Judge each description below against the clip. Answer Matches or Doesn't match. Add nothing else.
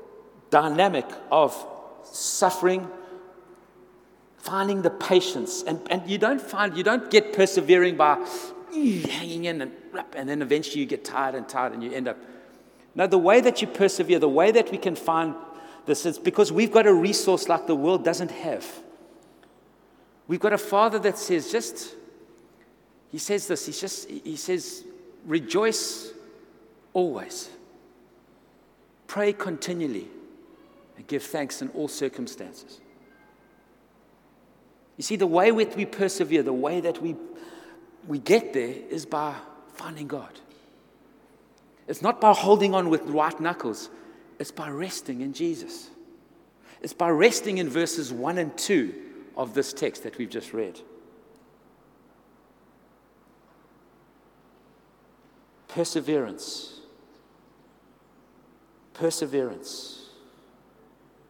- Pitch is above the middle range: Matches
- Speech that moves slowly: Matches